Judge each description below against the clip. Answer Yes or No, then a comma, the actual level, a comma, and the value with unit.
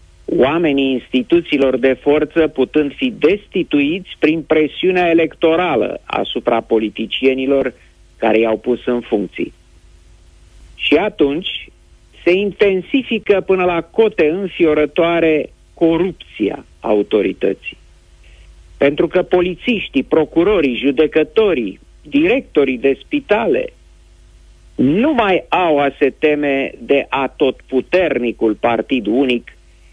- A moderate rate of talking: No, slow, 95 wpm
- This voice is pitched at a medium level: Yes, medium, 145 Hz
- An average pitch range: No, wide, 7.4 semitones